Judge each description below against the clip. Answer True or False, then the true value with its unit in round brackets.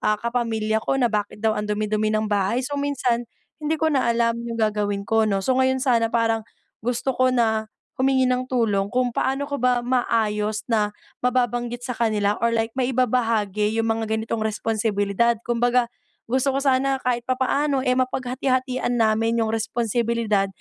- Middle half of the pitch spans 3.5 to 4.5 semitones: False (2.7 semitones)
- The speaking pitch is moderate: False (235 Hz)